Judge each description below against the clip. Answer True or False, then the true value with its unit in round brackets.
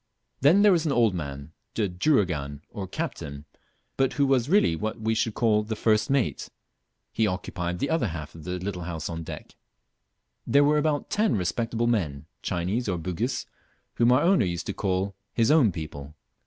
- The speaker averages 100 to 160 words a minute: False (180 wpm)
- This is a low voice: True (105 Hz)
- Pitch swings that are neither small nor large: False (7.0 semitones)